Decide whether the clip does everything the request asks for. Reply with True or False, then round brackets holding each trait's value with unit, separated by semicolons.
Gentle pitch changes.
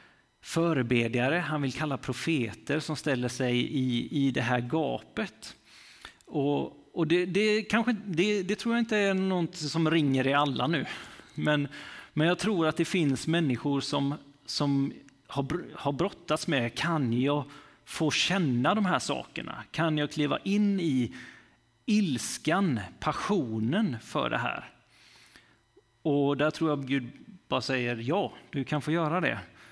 False (3.8 semitones)